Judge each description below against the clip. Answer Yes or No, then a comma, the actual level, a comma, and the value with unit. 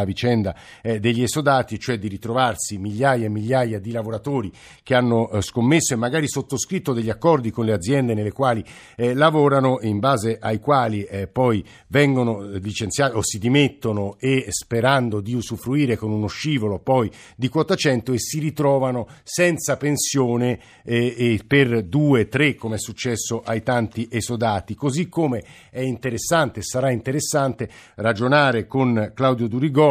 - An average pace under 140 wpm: No, average, 145 wpm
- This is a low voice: Yes, low, 120 Hz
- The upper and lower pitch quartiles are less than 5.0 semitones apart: Yes, average, 3.7 semitones